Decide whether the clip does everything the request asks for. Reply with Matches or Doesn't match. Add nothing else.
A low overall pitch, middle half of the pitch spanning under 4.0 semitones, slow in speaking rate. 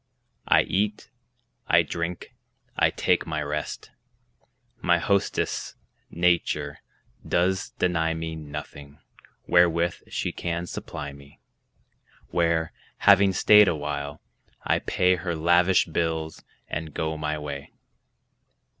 Matches